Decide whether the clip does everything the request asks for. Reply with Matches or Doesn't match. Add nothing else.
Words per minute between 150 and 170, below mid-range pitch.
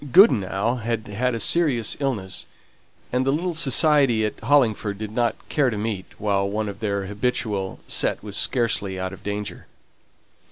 Matches